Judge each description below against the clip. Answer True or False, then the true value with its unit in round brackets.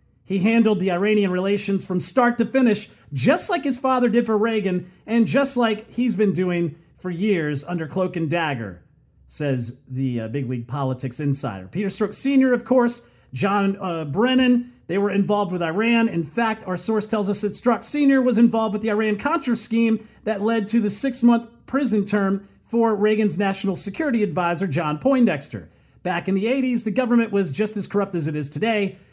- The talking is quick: False (185 wpm)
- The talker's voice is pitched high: True (205 Hz)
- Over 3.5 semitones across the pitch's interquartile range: True (4.9 semitones)